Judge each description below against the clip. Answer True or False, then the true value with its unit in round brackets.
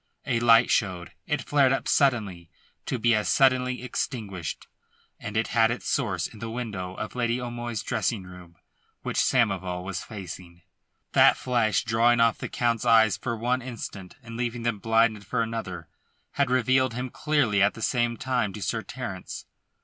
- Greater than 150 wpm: True (170 wpm)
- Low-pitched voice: True (115 Hz)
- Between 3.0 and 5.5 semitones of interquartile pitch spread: True (3.3 semitones)